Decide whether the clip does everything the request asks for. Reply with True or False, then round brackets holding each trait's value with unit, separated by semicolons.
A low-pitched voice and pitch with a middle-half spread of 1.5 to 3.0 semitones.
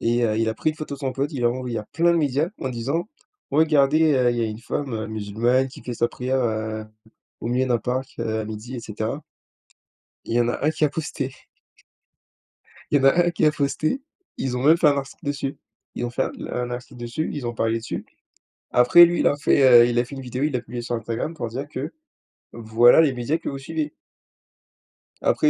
False (130 Hz; 3.6 semitones)